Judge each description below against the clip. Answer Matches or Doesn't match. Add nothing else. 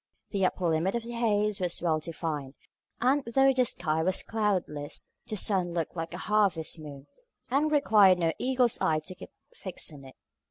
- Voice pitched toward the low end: Doesn't match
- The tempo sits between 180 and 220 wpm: Matches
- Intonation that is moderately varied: Doesn't match